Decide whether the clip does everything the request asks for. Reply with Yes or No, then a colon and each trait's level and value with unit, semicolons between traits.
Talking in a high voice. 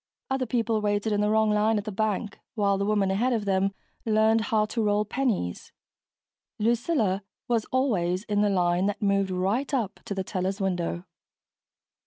Yes: high, 210 Hz